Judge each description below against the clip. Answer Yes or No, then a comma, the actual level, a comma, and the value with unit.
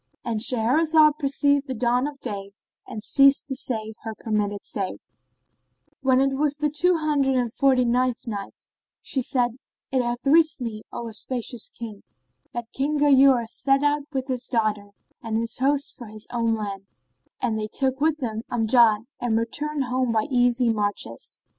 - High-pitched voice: Yes, high, 245 Hz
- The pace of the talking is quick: No, average, 165 wpm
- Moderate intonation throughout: Yes, average, 3.7 semitones